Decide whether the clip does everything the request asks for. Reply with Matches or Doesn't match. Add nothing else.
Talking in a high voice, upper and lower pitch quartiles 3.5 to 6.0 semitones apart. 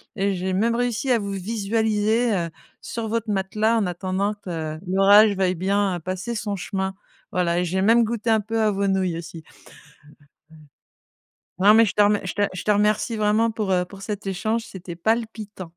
Doesn't match